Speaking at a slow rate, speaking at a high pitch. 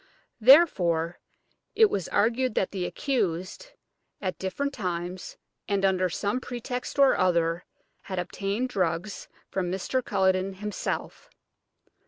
Yes: slow, 115 wpm; high, 195 Hz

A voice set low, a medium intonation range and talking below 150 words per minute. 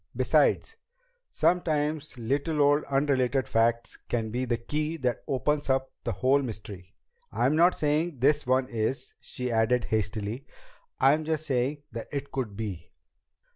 Yes: low, 130 Hz; average, 4.1 semitones; average, 140 wpm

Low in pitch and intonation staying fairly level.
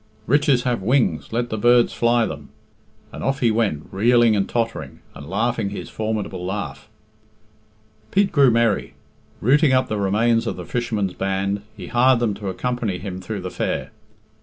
No: low, 115 Hz; average, 3.6 semitones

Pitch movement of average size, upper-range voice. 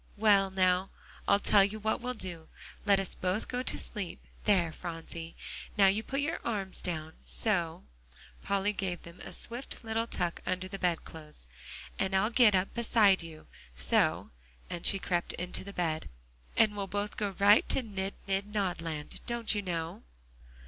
Yes: average, 3.1 semitones; high, 195 Hz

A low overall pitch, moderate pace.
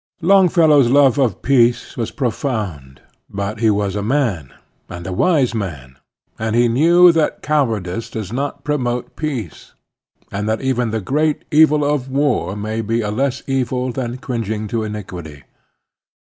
Yes: low, 120 Hz; average, 150 wpm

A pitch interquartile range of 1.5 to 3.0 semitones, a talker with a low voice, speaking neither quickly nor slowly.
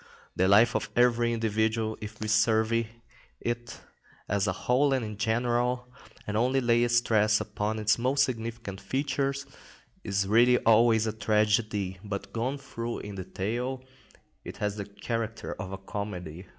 Yes: narrow, 2.5 semitones; low, 110 Hz; average, 150 wpm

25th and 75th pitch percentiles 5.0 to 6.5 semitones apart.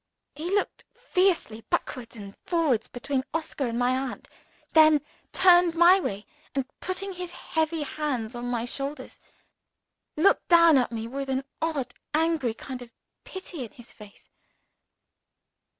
Yes: wide, 5.5 semitones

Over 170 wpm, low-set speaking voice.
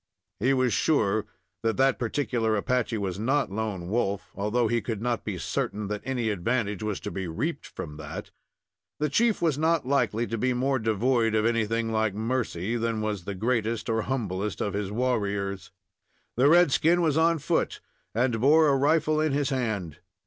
Yes: average, 180 wpm; low, 115 Hz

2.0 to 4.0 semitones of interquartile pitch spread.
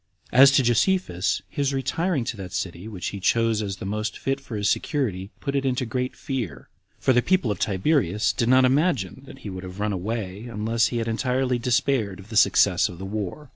No: average, 5.1 semitones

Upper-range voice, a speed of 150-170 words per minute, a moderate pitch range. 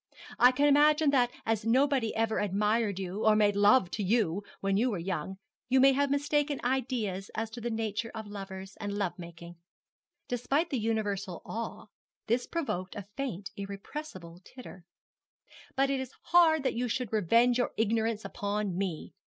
Yes: high, 220 Hz; average, 165 wpm; average, 4.7 semitones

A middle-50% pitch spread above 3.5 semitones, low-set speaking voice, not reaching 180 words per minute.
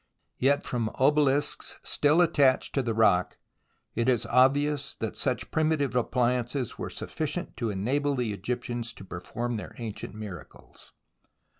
Yes: average, 3.9 semitones; low, 125 Hz; slow, 135 wpm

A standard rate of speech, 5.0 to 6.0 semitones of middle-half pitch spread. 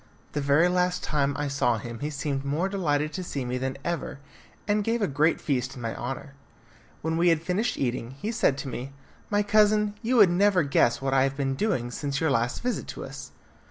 No: fast, 220 wpm; wide, 5.4 semitones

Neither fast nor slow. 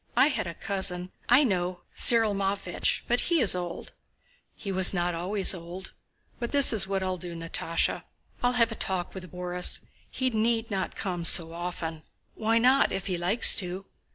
Yes: average, 180 wpm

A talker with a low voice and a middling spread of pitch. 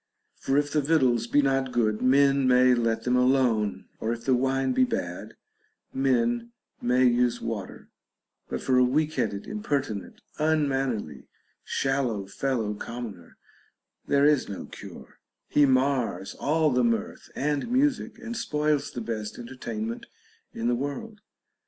Yes: low, 130 Hz; average, 3.4 semitones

